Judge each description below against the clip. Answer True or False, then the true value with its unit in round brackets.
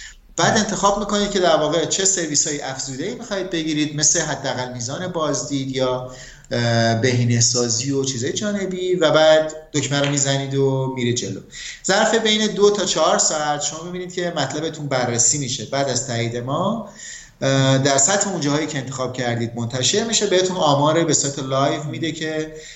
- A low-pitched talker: False (150 Hz)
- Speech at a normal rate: False (165 wpm)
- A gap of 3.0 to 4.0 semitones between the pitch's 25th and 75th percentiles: False (5.1 semitones)